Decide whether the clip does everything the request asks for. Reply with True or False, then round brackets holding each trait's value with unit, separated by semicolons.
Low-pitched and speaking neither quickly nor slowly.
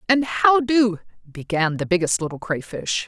False (195 Hz; 155 wpm)